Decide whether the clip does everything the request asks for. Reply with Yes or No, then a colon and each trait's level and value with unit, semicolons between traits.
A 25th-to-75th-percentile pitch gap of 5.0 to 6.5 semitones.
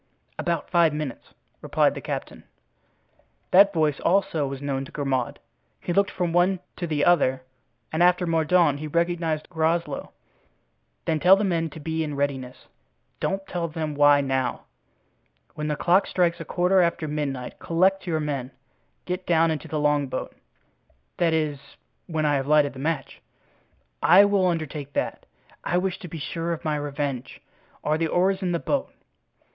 No: average, 3.2 semitones